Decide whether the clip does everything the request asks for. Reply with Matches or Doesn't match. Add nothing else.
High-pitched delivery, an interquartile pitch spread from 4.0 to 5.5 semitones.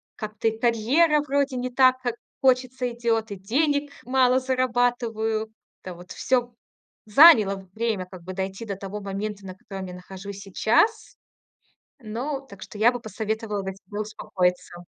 Matches